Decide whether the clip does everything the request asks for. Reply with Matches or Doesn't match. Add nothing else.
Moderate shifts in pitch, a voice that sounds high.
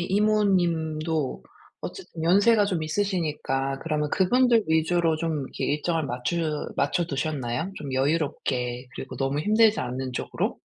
Doesn't match